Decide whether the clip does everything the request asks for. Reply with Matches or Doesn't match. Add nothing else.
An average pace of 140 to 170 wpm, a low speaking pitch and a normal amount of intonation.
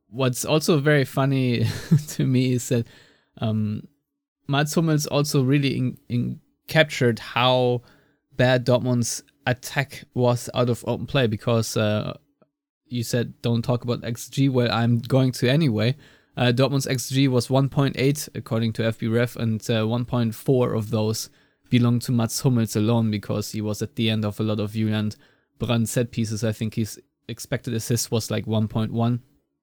Matches